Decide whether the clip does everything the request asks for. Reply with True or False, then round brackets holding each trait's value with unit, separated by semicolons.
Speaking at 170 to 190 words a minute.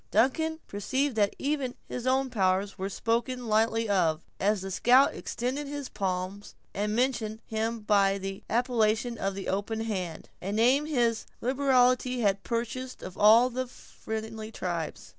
False (145 wpm)